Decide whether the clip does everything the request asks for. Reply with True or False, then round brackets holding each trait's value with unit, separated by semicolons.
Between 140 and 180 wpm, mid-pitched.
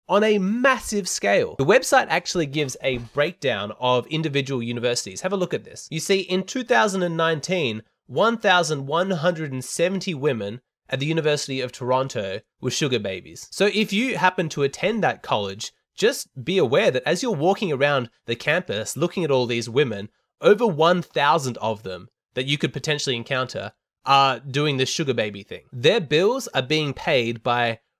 True (165 wpm; 145 Hz)